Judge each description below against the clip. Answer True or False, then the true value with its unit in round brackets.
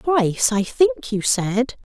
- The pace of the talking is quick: False (155 wpm)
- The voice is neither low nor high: False (240 Hz)